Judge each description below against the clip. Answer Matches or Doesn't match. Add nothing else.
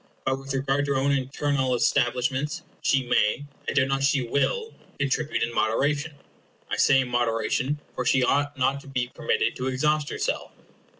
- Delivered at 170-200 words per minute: Matches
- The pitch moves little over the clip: Matches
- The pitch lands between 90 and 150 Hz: Matches